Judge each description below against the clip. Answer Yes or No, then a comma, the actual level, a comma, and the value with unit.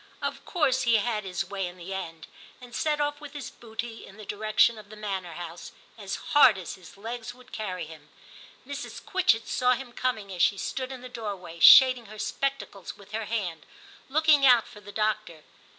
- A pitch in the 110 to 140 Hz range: No, high, 215 Hz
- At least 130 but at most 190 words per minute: No, average, 200 wpm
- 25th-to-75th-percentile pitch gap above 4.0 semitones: Yes, average, 4.7 semitones